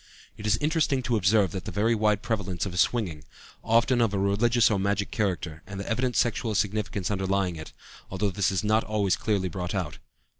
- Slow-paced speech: No, average, 190 wpm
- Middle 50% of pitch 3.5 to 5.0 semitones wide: No, average, 2.9 semitones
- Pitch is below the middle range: Yes, low, 100 Hz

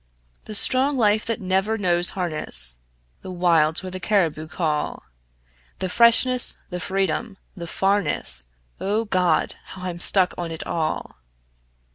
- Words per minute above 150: No, slow, 135 wpm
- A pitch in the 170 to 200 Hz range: Yes, medium, 185 Hz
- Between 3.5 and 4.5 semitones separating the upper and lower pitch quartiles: Yes, average, 3.8 semitones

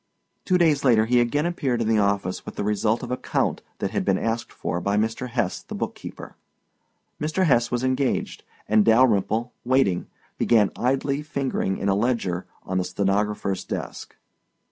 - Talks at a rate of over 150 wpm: Yes, average, 170 wpm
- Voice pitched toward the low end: Yes, low, 115 Hz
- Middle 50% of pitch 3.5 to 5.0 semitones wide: Yes, average, 4.4 semitones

